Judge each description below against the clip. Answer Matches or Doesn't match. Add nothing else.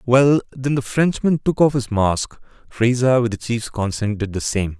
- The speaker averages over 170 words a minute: Matches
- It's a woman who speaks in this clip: Doesn't match